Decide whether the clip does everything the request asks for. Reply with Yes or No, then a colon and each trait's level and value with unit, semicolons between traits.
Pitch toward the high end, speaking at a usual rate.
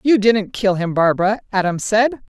Yes: high, 205 Hz; average, 175 wpm